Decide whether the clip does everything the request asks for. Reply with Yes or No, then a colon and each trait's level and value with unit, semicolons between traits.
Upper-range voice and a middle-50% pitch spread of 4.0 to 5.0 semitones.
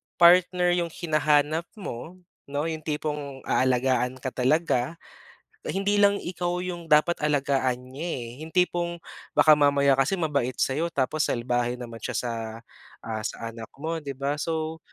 No: medium, 150 Hz; average, 4.7 semitones